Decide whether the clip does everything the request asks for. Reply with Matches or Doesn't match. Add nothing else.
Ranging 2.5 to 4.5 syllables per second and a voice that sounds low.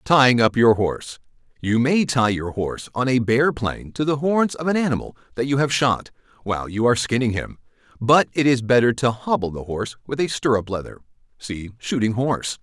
Doesn't match